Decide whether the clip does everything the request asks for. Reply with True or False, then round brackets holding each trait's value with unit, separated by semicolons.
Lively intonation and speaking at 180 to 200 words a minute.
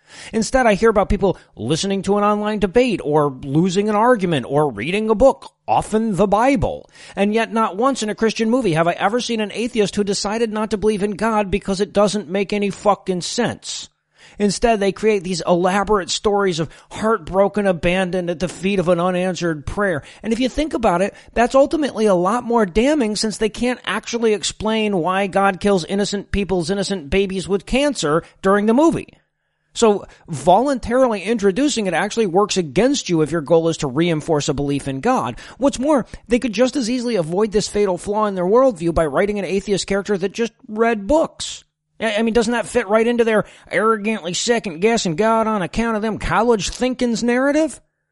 False (3.5 semitones; 190 wpm)